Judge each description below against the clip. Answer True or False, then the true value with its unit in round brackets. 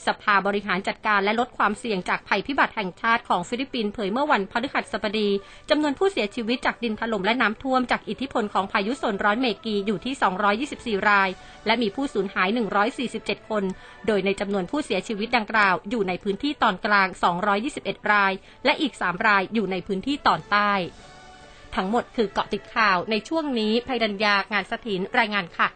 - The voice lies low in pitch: False (215 Hz)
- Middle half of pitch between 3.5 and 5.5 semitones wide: False (3.1 semitones)